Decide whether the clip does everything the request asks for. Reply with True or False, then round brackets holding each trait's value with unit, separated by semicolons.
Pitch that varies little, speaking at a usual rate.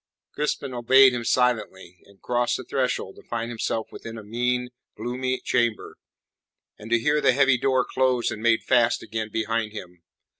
True (2.3 semitones; 165 wpm)